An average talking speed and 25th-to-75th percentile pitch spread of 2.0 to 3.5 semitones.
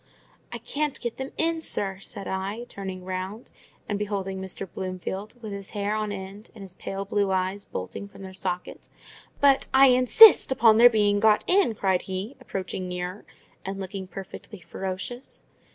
Yes: average, 170 wpm; average, 3.0 semitones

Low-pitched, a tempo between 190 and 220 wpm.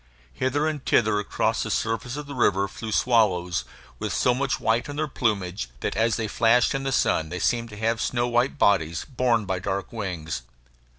Yes: low, 115 Hz; average, 195 wpm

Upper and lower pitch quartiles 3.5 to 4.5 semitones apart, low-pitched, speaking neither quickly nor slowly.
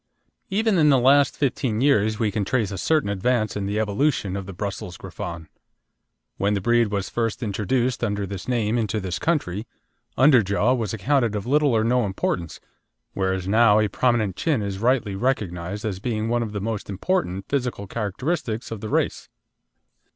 Yes: average, 4.0 semitones; low, 110 Hz; average, 175 wpm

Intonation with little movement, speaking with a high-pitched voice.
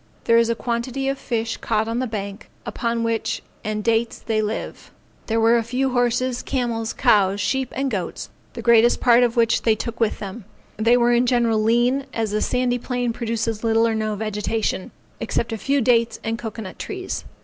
Yes: narrow, 1.7 semitones; high, 230 Hz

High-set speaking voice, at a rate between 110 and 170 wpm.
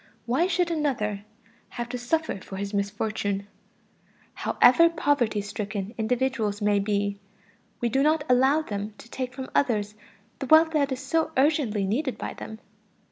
Yes: high, 240 Hz; average, 150 wpm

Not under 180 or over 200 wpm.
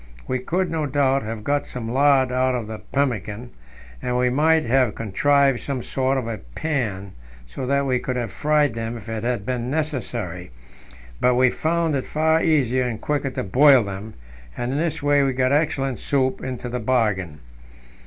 Yes: average, 185 wpm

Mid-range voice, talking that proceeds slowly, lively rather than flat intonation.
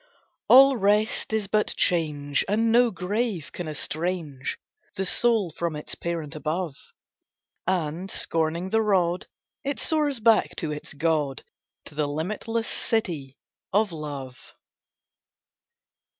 Yes: medium, 175 Hz; slow, 120 wpm; wide, 5.9 semitones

